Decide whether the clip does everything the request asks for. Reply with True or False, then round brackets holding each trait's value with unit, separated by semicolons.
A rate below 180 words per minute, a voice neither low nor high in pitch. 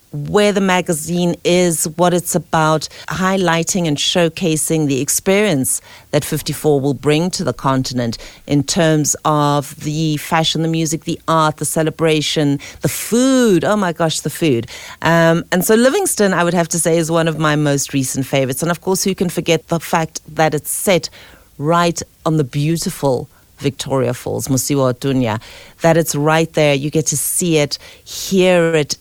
True (170 wpm; 160 Hz)